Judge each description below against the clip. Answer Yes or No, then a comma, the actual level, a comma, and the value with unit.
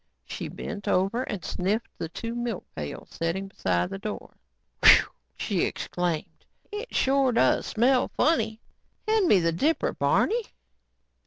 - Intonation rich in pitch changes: Yes, wide, 6.9 semitones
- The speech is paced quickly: No, average, 145 wpm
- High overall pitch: Yes, high, 220 Hz